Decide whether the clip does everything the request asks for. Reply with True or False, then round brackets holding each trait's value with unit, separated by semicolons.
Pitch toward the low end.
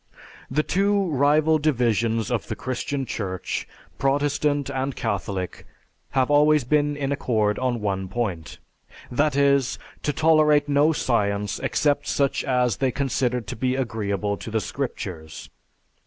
True (130 Hz)